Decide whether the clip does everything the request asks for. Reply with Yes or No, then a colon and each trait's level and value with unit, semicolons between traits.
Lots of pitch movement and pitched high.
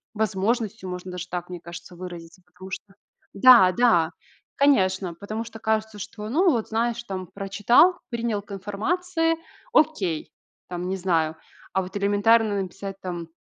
No: average, 4.1 semitones; high, 200 Hz